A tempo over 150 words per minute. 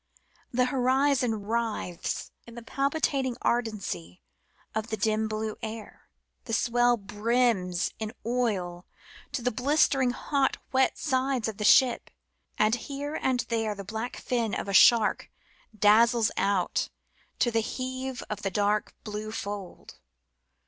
No: slow, 135 wpm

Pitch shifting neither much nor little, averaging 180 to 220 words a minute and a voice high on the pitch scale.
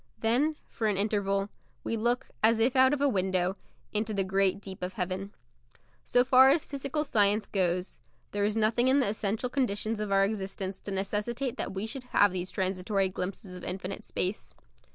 Yes: average, 3.7 semitones; average, 185 wpm; high, 205 Hz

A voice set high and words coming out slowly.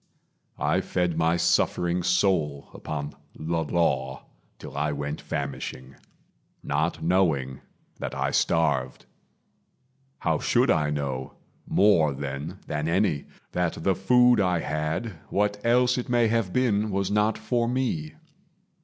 No: very low, 85 Hz; slow, 125 wpm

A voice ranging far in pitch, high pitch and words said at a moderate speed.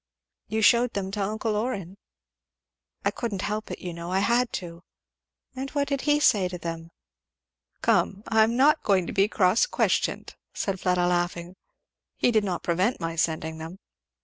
No: average, 4.5 semitones; high, 195 Hz; average, 165 wpm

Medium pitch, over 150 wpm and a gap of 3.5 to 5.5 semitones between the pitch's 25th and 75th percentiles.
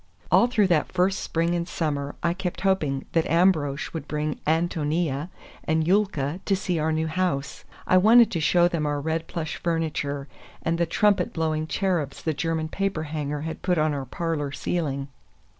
No: medium, 160 Hz; average, 175 wpm; average, 3.0 semitones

